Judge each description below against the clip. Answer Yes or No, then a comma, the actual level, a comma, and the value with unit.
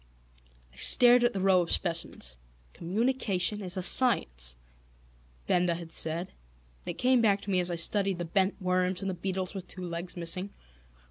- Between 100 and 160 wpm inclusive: No, average, 180 wpm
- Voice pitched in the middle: Yes, medium, 180 Hz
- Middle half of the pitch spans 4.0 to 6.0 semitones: No, average, 2.7 semitones